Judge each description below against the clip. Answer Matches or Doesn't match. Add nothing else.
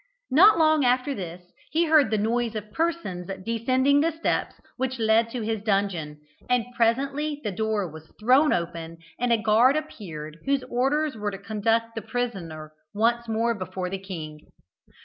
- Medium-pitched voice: Doesn't match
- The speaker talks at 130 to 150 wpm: Doesn't match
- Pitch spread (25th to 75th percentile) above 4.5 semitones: Matches